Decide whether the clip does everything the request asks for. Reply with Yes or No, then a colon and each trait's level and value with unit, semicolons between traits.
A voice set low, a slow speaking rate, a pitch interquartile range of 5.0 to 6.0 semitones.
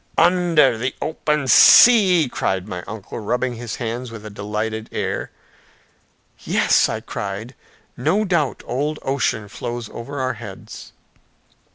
Yes: low, 120 Hz; slow, 130 wpm; average, 5.3 semitones